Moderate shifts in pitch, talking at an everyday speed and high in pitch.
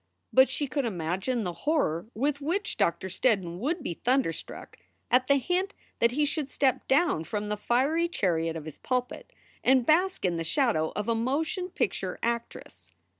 No: wide, 7.6 semitones; average, 175 wpm; very high, 250 Hz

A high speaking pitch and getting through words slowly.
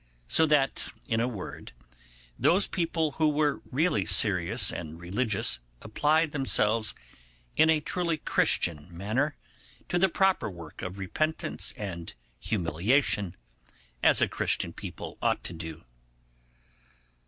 No: low, 115 Hz; slow, 120 wpm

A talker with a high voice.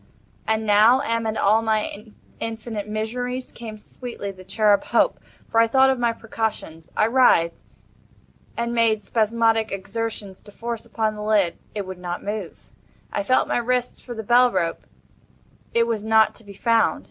Yes: high, 220 Hz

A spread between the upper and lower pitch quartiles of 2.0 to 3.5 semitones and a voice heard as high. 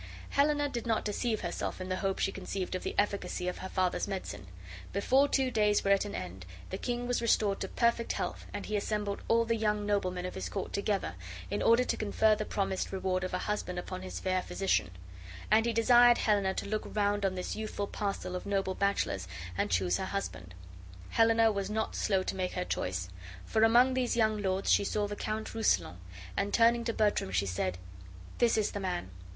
Yes: average, 3.1 semitones; high, 205 Hz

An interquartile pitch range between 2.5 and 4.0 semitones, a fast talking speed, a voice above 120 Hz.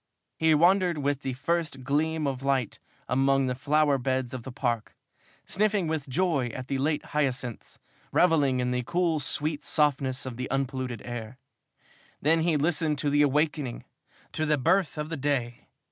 No: average, 3.3 semitones; average, 165 wpm; medium, 140 Hz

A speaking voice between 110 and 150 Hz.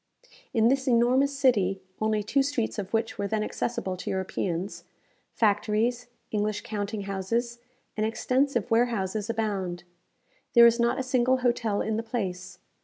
No: high, 220 Hz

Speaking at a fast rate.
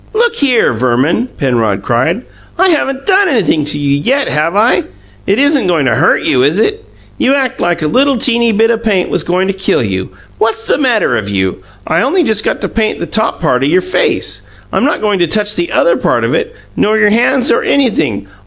Yes: fast, 220 wpm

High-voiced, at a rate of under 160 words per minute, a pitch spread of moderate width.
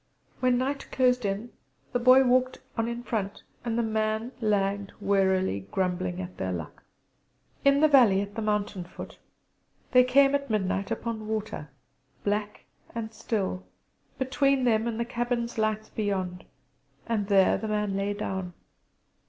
Yes: high, 215 Hz; average, 150 wpm; average, 3.7 semitones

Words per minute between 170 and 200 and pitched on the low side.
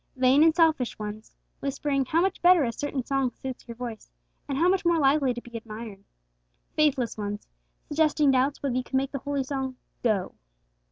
No: average, 185 wpm; very high, 265 Hz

